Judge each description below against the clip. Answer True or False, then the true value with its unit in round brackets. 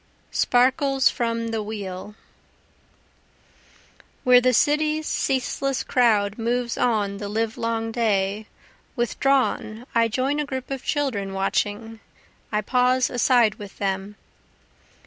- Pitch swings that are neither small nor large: True (3.5 semitones)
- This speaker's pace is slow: True (110 wpm)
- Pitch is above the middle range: True (230 Hz)